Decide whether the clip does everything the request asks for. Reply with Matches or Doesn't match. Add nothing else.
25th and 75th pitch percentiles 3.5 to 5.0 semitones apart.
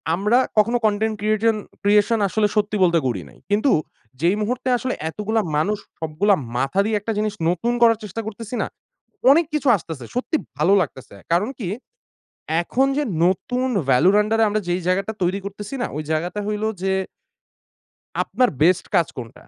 Matches